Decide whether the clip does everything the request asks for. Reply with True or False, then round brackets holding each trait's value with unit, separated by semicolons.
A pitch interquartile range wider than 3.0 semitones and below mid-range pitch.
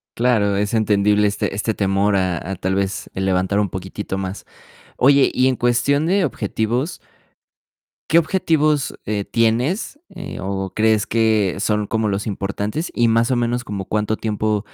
True (3.6 semitones; 105 Hz)